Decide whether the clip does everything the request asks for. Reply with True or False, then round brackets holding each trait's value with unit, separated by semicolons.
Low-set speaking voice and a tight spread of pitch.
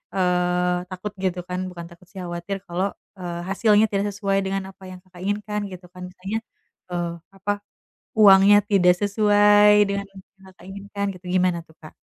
False (190 Hz; 2.1 semitones)